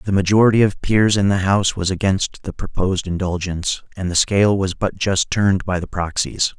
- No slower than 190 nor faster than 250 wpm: Yes, average, 200 wpm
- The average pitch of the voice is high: No, very low, 95 Hz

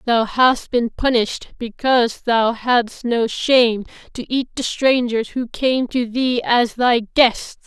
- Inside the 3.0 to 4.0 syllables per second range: Yes, 3.8 syllables/s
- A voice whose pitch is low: No, high, 240 Hz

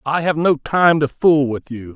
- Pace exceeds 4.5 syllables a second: No, 4.4 syllables/s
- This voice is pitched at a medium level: Yes, medium, 145 Hz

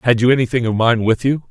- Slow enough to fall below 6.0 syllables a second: No, 6.5 syllables/s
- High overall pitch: No, low, 120 Hz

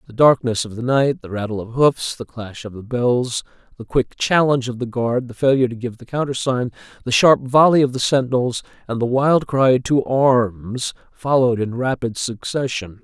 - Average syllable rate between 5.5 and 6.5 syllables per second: No, 4.9 syllables/s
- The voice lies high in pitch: No, low, 125 Hz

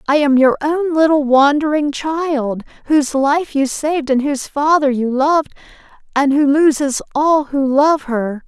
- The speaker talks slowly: No, average, 165 wpm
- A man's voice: No, female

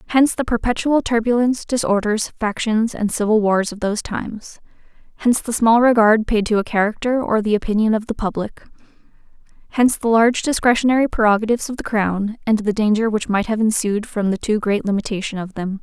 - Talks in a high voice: Yes, high, 220 Hz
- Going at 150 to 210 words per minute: Yes, average, 180 wpm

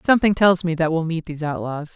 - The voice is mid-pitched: Yes, medium, 170 Hz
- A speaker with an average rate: No, fast, 245 wpm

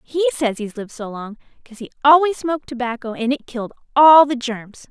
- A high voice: Yes, very high, 255 Hz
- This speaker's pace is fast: Yes, fast, 210 wpm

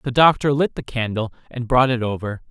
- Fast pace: Yes, fast, 215 wpm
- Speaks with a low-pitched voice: Yes, low, 125 Hz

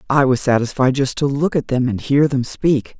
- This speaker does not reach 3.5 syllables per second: No, 5.0 syllables/s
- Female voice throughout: Yes, female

